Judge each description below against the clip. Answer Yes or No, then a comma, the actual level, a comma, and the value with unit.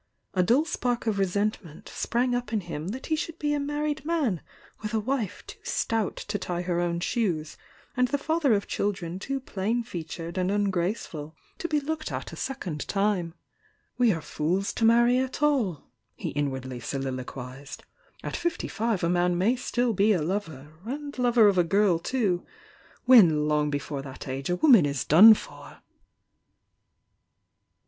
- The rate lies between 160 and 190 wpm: Yes, average, 175 wpm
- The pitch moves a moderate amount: No, wide, 6.8 semitones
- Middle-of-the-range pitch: No, high, 200 Hz